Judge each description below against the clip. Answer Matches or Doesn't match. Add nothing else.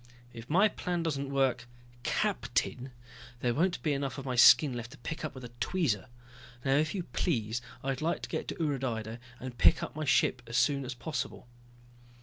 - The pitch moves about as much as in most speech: Matches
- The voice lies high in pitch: Doesn't match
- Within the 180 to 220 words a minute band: Matches